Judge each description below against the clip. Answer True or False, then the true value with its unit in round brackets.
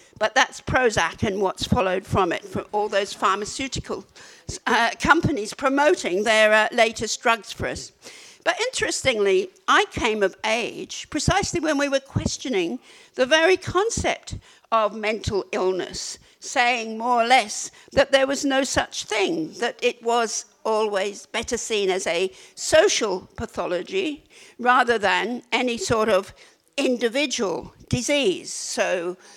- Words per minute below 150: True (135 wpm)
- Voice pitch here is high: True (245 Hz)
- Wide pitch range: True (6.0 semitones)